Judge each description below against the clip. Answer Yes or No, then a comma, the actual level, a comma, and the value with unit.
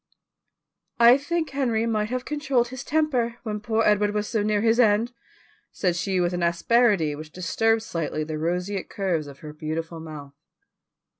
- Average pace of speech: Yes, average, 165 wpm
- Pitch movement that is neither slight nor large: No, wide, 5.7 semitones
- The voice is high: Yes, high, 210 Hz